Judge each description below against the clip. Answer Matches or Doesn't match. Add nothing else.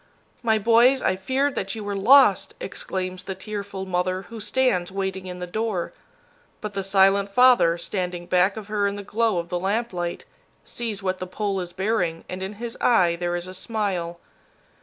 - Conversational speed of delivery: Matches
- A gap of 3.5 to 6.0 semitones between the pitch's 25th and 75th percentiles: Doesn't match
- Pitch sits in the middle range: Doesn't match